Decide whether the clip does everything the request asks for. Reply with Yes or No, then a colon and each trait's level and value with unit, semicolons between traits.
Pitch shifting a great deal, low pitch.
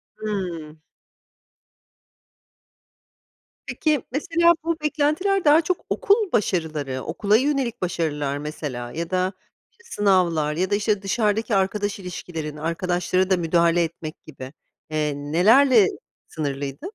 No: wide, 6.8 semitones; medium, 185 Hz